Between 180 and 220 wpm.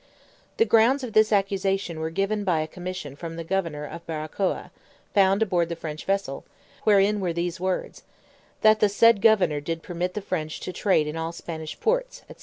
Yes: average, 190 wpm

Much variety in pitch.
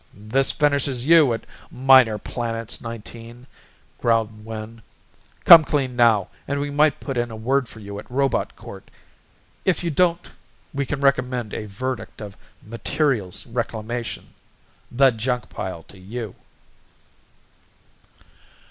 No: average, 3.7 semitones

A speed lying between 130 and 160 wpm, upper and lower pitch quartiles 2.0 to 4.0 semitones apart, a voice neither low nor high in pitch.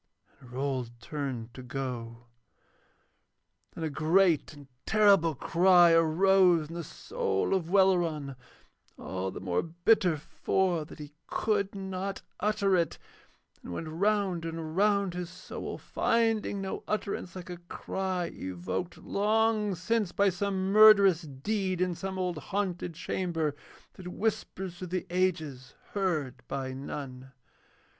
No: slow, 135 wpm; average, 4.6 semitones; medium, 175 Hz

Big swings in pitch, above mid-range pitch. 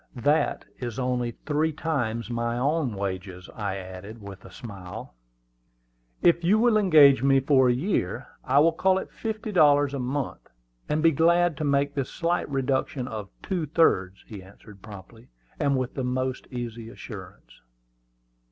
No: wide, 5.7 semitones; low, 130 Hz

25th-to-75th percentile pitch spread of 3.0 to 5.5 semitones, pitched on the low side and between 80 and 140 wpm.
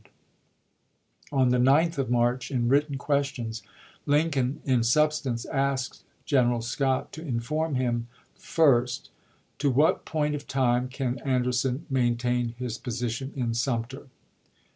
No: narrow, 2.6 semitones; low, 130 Hz; slow, 135 wpm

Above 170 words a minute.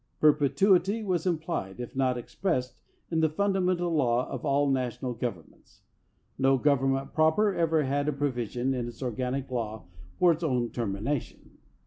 No: average, 155 wpm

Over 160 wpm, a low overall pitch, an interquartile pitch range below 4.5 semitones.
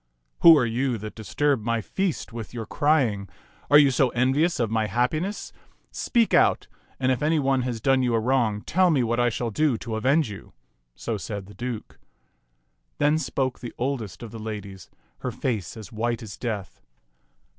Yes: average, 190 wpm; low, 120 Hz; average, 3.9 semitones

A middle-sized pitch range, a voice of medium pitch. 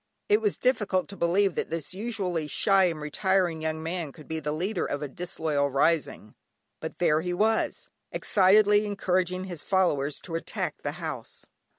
Yes: average, 3.8 semitones; medium, 180 Hz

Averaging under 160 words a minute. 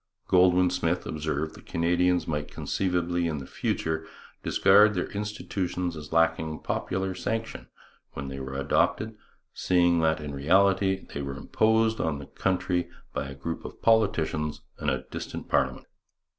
Yes: average, 145 wpm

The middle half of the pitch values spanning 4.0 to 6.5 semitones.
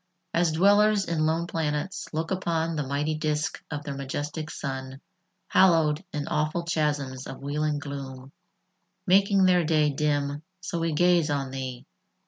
No: average, 2.9 semitones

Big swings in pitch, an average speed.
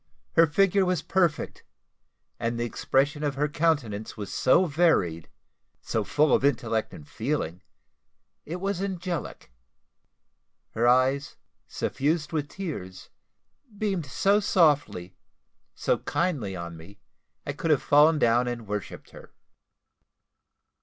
No: wide, 6.6 semitones; slow, 120 wpm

